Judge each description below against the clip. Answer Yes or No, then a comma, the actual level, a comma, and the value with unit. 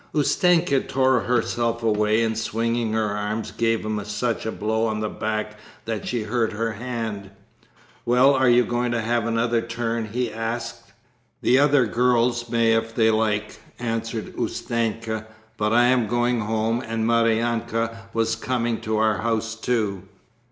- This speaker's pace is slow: No, average, 155 wpm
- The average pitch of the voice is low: Yes, low, 115 Hz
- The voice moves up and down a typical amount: No, narrow, 1.4 semitones